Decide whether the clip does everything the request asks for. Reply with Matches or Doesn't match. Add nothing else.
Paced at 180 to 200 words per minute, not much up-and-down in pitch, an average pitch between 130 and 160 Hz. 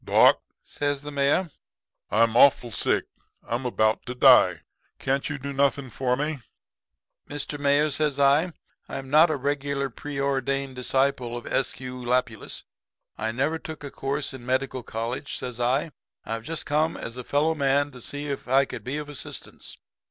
Doesn't match